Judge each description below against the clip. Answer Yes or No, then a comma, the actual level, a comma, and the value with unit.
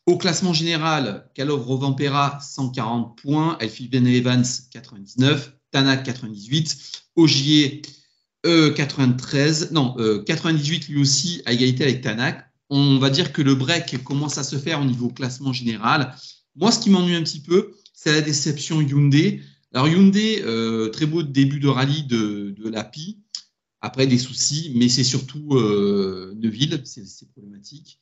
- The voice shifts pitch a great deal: No, average, 3.7 semitones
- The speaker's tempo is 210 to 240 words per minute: No, average, 155 wpm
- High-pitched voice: No, medium, 140 Hz